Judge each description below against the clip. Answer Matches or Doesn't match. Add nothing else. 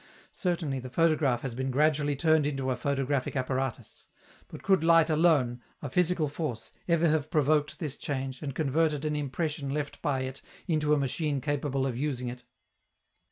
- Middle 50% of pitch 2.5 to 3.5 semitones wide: Matches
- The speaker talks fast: Doesn't match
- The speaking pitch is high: Doesn't match